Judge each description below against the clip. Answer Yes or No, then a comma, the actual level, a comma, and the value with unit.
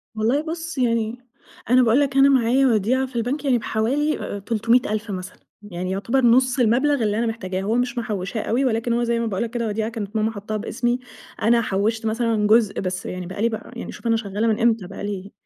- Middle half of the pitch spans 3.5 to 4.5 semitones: No, average, 2.8 semitones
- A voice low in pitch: No, high, 230 Hz